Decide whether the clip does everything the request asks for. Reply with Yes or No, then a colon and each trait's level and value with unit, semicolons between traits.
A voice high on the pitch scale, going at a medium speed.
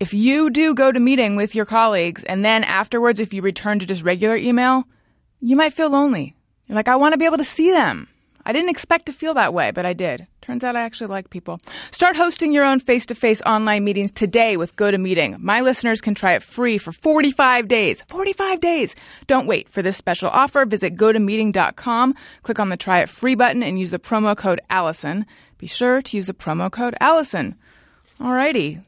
No: high, 230 Hz; fast, 215 wpm